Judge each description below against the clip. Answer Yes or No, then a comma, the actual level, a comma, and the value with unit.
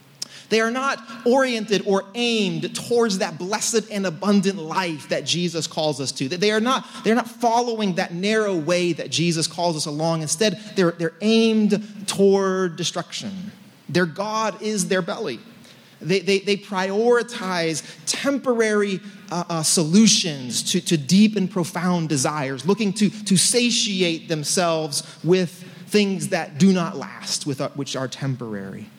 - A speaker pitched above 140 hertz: Yes, high, 190 Hz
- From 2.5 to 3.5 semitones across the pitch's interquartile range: No, average, 4.1 semitones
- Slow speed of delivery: No, average, 145 wpm